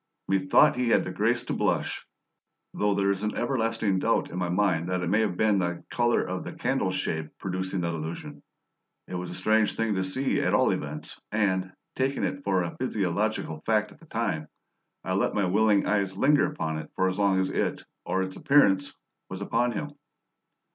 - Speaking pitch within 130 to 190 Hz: No, low, 100 Hz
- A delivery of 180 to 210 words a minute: Yes, average, 195 wpm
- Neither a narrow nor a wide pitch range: Yes, average, 3.1 semitones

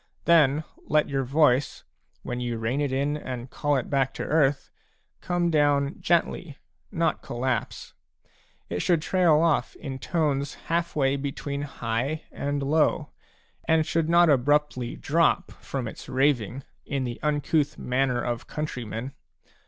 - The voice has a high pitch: No, medium, 140 Hz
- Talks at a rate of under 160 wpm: Yes, average, 140 wpm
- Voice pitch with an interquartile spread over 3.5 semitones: No, average, 3.0 semitones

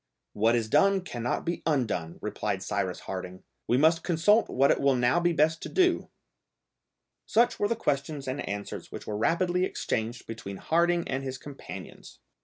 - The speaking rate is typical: Yes, average, 170 wpm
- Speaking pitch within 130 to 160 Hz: Yes, medium, 140 Hz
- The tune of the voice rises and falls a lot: Yes, wide, 6.7 semitones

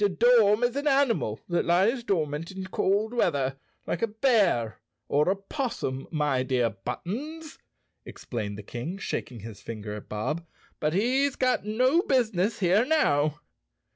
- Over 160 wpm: No, average, 150 wpm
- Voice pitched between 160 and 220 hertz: Yes, high, 190 Hz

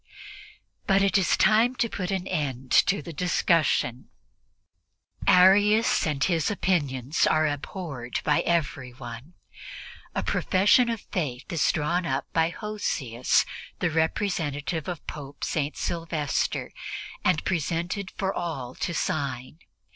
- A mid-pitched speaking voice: Yes, medium, 165 Hz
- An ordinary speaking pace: No, slow, 120 wpm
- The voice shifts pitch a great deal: No, average, 5.0 semitones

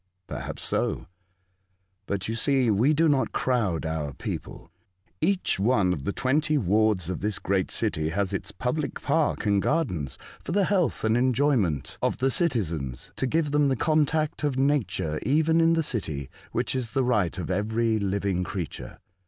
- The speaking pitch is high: No, low, 115 Hz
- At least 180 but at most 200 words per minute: No, average, 170 wpm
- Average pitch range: No, wide, 7.8 semitones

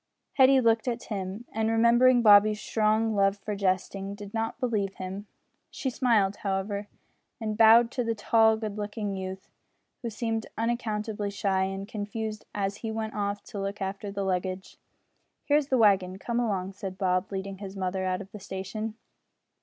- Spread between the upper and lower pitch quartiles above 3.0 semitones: No, narrow, 2.4 semitones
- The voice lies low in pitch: No, high, 205 Hz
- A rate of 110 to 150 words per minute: No, average, 170 wpm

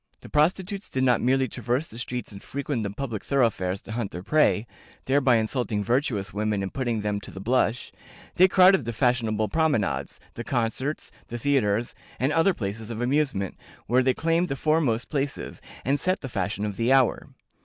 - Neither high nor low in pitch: No, low, 120 Hz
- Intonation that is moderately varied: Yes, average, 4.7 semitones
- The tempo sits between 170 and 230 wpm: Yes, average, 185 wpm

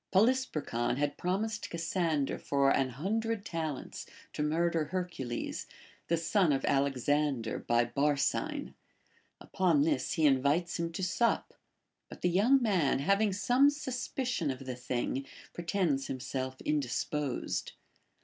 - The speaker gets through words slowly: Yes, slow, 130 wpm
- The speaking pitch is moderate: Yes, medium, 160 Hz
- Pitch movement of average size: No, wide, 5.9 semitones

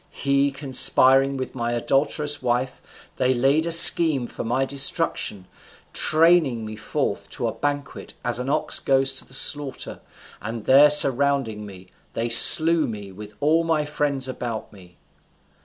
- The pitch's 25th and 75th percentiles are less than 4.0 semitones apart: Yes, average, 3.6 semitones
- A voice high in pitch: No, low, 135 Hz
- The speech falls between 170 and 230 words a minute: No, average, 150 wpm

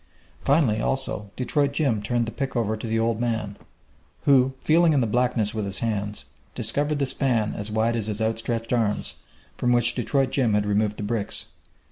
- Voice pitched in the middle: No, low, 115 Hz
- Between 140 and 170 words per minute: No, average, 185 wpm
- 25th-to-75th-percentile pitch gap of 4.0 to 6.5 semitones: No, average, 3.5 semitones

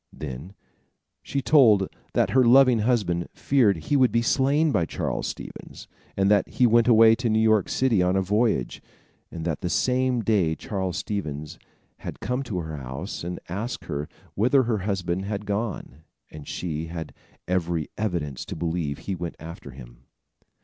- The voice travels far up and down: Yes, wide, 6.0 semitones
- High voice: No, low, 100 Hz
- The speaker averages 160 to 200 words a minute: Yes, average, 170 wpm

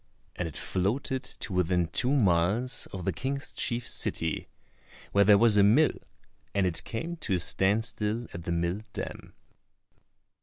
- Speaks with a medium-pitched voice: No, low, 100 Hz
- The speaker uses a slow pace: No, average, 160 wpm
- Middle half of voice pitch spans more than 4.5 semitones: Yes, average, 5.1 semitones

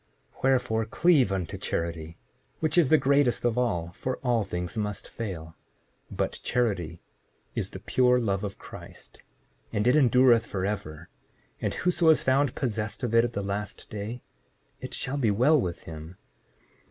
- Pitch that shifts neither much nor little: Yes, average, 4.9 semitones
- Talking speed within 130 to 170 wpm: Yes, average, 160 wpm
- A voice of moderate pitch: No, low, 110 Hz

